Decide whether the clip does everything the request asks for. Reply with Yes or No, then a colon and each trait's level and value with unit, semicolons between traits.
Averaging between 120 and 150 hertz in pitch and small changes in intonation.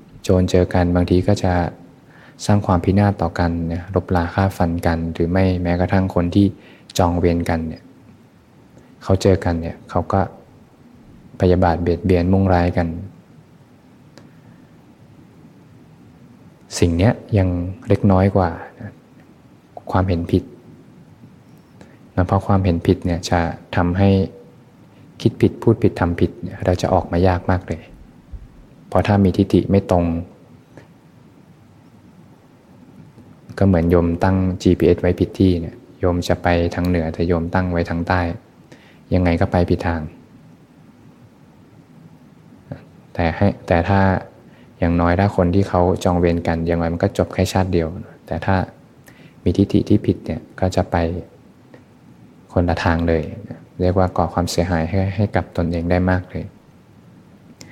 No: very low, 90 Hz; narrow, 2.0 semitones